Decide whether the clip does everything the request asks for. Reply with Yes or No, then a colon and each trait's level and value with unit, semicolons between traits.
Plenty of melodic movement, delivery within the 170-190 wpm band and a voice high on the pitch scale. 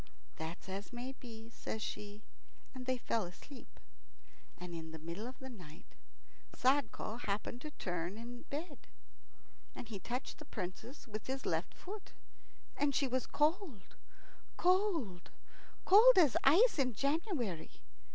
No: wide, 6.3 semitones; average, 140 wpm; high, 245 Hz